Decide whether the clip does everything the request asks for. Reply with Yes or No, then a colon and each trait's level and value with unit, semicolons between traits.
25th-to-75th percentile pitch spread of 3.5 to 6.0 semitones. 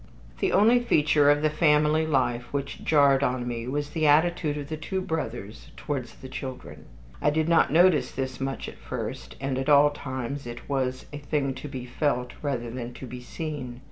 No: average, 3.0 semitones